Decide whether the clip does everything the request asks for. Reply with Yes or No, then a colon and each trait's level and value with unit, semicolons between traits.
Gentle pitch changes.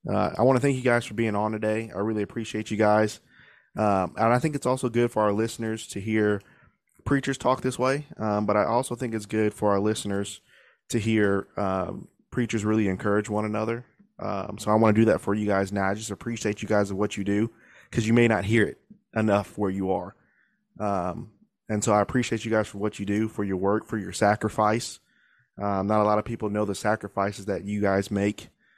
Yes: narrow, 2.1 semitones